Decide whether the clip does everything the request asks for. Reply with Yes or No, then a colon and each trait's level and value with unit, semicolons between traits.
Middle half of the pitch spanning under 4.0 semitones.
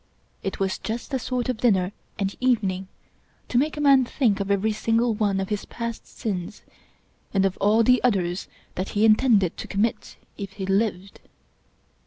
Yes: average, 3.5 semitones